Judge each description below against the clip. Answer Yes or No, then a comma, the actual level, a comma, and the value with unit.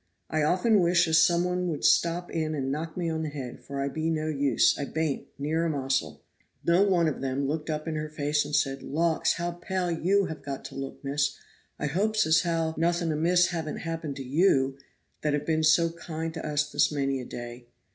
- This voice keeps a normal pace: No, fast, 220 wpm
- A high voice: No, medium, 155 Hz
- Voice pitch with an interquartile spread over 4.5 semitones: No, average, 3.0 semitones